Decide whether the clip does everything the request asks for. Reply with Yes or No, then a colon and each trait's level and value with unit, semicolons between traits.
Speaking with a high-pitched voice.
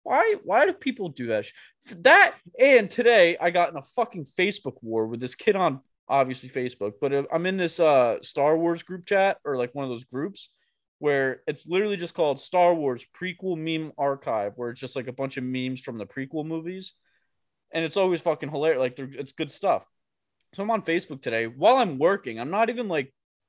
No: medium, 155 Hz